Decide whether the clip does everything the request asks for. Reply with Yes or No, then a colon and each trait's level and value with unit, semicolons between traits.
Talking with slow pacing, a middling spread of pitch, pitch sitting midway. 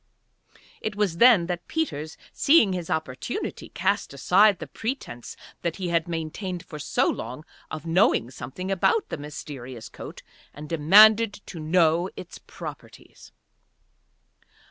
Yes: slow, 130 wpm; average, 4.5 semitones; medium, 170 Hz